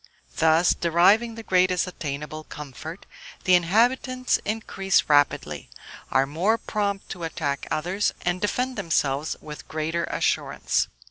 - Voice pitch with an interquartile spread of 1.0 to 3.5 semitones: No, average, 4.8 semitones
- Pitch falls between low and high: Yes, medium, 175 Hz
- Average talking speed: No, slow, 120 wpm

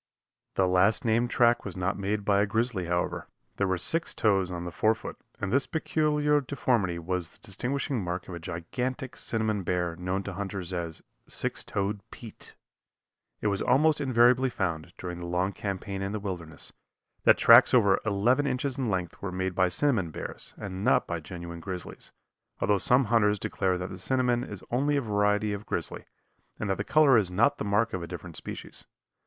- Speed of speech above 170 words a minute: Yes, average, 190 wpm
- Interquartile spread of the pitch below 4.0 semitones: No, average, 4.8 semitones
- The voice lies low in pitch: Yes, low, 100 Hz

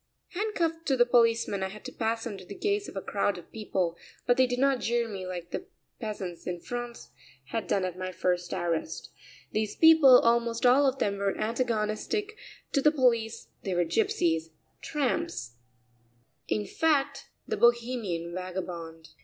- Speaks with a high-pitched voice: Yes, high, 225 Hz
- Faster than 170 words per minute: No, average, 165 wpm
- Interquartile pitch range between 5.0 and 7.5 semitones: Yes, wide, 5.5 semitones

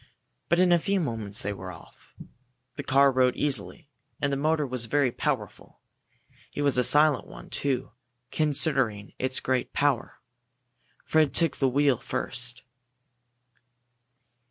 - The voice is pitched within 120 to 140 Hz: Yes, low, 135 Hz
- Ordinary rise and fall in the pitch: Yes, average, 3.1 semitones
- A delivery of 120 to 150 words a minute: Yes, slow, 135 wpm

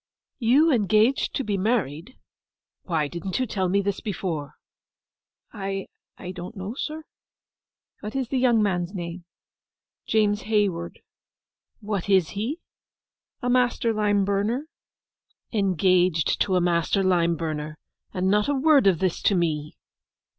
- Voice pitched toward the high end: Yes, high, 195 Hz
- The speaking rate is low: Yes, slow, 130 wpm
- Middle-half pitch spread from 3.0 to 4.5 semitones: Yes, average, 4.0 semitones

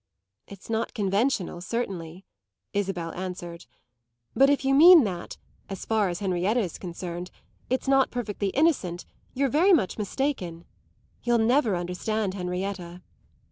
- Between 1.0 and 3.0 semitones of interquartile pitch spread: No, wide, 5.6 semitones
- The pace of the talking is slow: Yes, slow, 130 wpm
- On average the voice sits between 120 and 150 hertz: No, high, 200 Hz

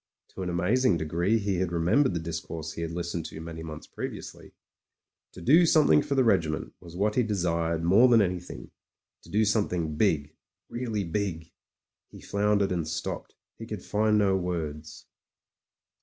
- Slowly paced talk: No, average, 170 wpm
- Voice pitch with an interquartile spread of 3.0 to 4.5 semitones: Yes, average, 4.2 semitones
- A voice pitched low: Yes, very low, 90 Hz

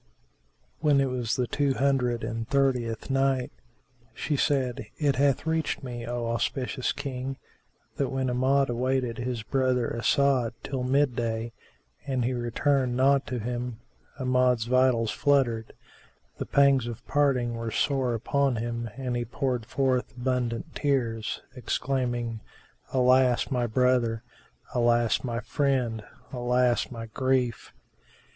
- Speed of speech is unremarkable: No, slow, 130 wpm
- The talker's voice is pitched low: Yes, low, 125 Hz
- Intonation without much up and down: Yes, narrow, 2.2 semitones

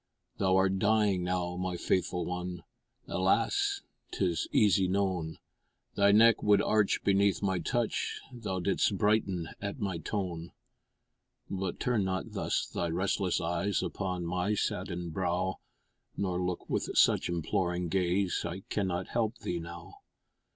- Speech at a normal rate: No, slow, 130 wpm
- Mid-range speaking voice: No, very low, 95 Hz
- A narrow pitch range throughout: Yes, narrow, 2.3 semitones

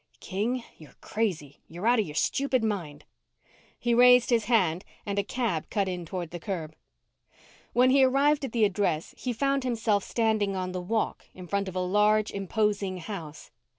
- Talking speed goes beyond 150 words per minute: Yes, average, 180 wpm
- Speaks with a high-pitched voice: Yes, high, 205 Hz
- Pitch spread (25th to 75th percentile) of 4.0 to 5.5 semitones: Yes, average, 4.5 semitones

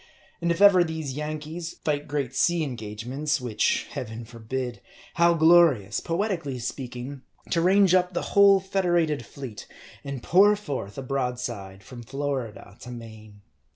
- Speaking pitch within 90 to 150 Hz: Yes, medium, 140 Hz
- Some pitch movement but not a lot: No, wide, 5.9 semitones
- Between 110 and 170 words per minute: Yes, average, 140 wpm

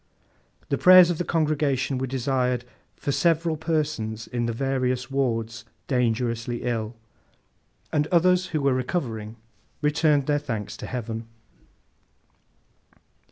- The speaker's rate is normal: No, slow, 115 wpm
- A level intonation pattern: No, average, 4.4 semitones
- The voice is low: Yes, low, 130 Hz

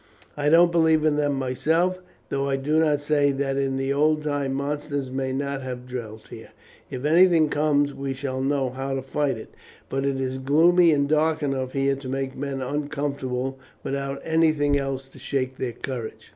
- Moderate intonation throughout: No, narrow, 1.9 semitones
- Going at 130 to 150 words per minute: No, average, 185 wpm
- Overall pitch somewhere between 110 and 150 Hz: Yes, medium, 140 Hz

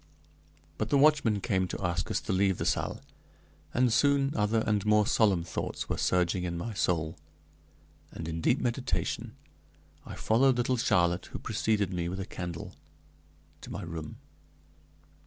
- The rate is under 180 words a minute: Yes, average, 155 wpm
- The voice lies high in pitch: No, low, 100 Hz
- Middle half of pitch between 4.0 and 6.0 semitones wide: Yes, average, 5.0 semitones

